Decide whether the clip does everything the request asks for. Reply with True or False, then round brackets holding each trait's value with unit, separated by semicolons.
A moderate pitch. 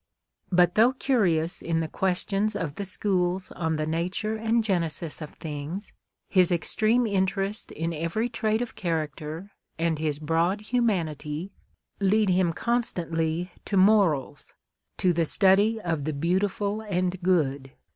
True (180 Hz)